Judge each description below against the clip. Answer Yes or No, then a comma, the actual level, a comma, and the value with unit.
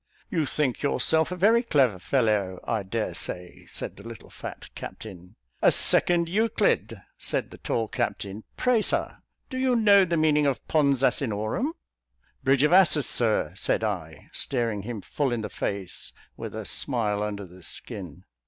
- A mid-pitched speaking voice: No, low, 125 Hz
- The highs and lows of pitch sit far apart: Yes, wide, 7.5 semitones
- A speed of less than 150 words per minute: No, average, 160 wpm